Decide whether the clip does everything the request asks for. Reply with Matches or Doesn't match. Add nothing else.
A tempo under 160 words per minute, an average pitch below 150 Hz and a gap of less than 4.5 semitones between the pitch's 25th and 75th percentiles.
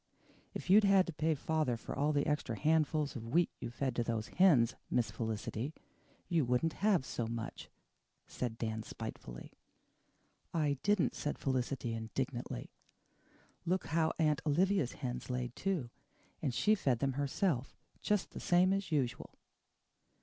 Doesn't match